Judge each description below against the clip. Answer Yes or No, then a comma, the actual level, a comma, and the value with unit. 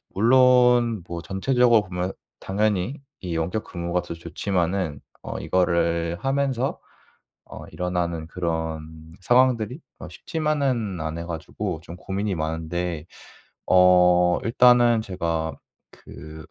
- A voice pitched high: No, very low, 90 Hz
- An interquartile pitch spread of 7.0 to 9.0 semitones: No, wide, 5.6 semitones